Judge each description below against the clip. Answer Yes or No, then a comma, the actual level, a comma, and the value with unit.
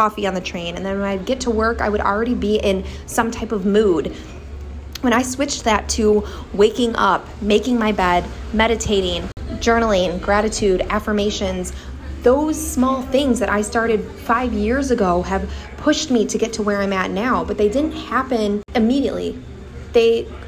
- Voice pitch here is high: Yes, high, 215 Hz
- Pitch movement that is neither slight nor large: Yes, average, 3.3 semitones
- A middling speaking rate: Yes, average, 175 wpm